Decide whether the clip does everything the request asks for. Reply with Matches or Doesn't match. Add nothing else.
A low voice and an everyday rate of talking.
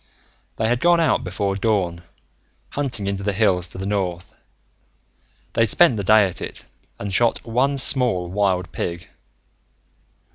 Matches